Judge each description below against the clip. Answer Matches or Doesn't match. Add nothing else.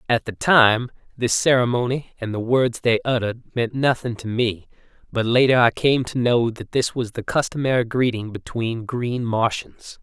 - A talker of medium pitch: Doesn't match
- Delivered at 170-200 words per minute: Matches